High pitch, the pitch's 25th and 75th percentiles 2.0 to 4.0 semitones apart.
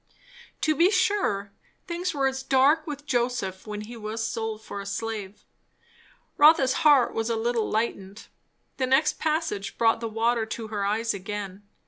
No: high, 230 Hz; average, 4.7 semitones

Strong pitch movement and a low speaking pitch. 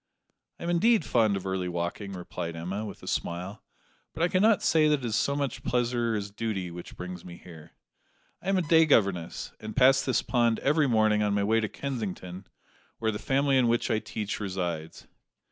Yes: wide, 6.5 semitones; low, 110 Hz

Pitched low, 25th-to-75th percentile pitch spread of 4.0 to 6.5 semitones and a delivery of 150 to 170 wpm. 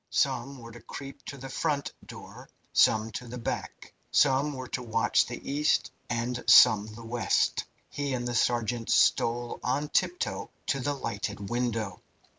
No: low, 120 Hz; average, 2.9 semitones; average, 160 wpm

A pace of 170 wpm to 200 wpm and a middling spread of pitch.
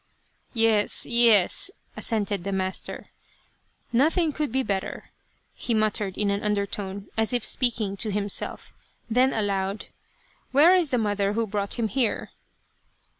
No: average, 155 wpm; average, 3.3 semitones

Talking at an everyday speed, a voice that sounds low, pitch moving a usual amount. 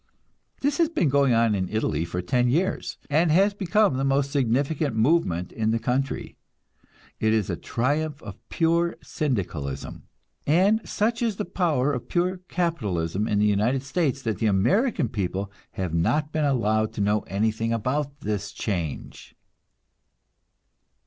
No: average, 150 wpm; low, 130 Hz; wide, 7.1 semitones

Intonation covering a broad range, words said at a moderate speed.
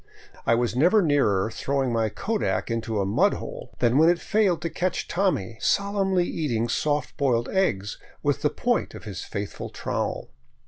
Yes: wide, 7.9 semitones; average, 170 wpm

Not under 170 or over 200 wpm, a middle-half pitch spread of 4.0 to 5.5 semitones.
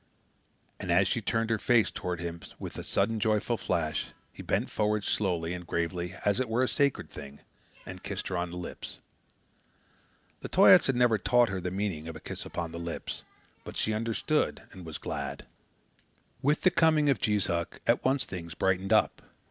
Yes: average, 190 wpm; average, 4.8 semitones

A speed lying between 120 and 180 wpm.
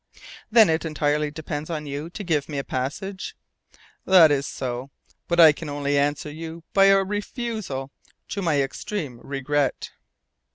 Yes: average, 155 wpm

